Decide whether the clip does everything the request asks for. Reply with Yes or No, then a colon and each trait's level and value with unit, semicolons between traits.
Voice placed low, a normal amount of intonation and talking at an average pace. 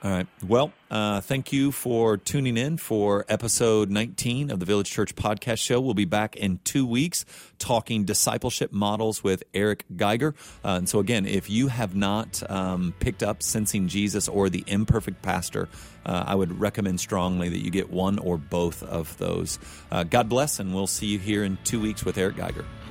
Yes: low, 105 Hz; average, 3.5 semitones; average, 195 wpm